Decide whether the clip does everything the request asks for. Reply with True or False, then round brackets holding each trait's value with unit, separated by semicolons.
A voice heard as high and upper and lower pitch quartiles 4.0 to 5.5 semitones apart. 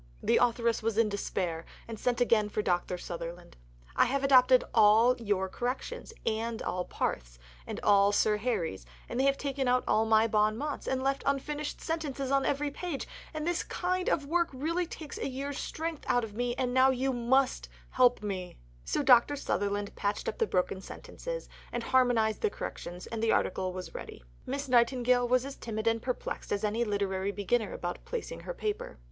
True (245 Hz; 4.7 semitones)